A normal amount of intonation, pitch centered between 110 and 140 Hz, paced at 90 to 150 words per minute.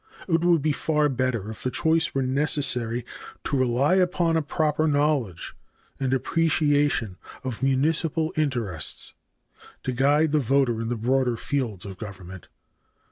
Yes: average, 4.3 semitones; low, 135 Hz; average, 140 wpm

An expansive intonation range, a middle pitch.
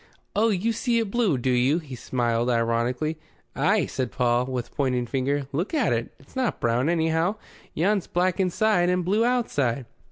Yes: wide, 7.7 semitones; medium, 155 Hz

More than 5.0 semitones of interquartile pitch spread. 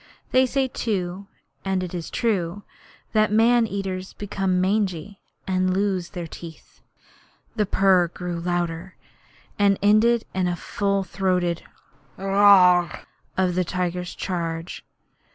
No: narrow, 2.4 semitones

